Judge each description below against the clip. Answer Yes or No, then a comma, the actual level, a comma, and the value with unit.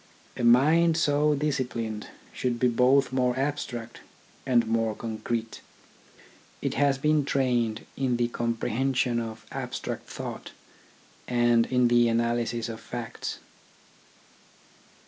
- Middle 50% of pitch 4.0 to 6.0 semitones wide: No, narrow, 2.5 semitones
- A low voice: Yes, low, 120 Hz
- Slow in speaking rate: Yes, slow, 110 wpm